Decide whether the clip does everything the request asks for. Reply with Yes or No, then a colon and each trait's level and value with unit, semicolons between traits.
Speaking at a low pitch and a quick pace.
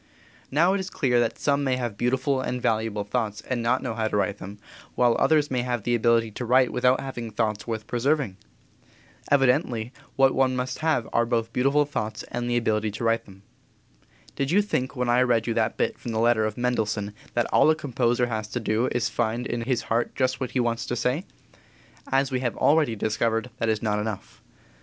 Yes: low, 120 Hz; fast, 215 wpm